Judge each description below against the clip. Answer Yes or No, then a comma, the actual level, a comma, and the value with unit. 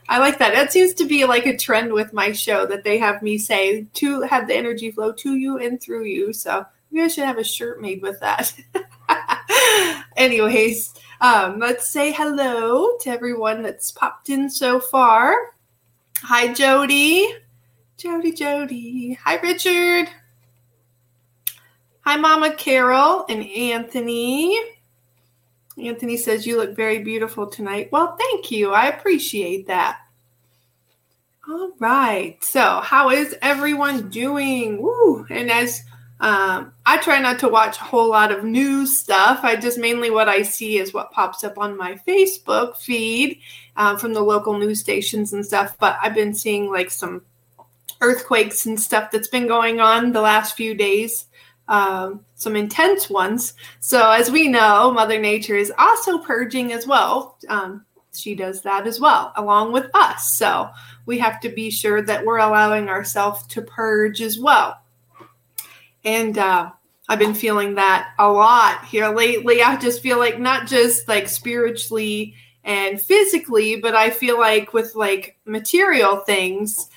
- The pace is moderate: Yes, average, 155 wpm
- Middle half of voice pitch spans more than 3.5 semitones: Yes, average, 4.3 semitones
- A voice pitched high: Yes, high, 225 Hz